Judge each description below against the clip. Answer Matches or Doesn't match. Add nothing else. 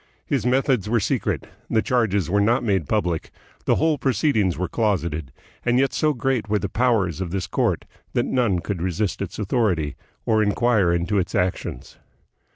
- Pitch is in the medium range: Doesn't match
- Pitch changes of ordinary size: Matches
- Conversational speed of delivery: Matches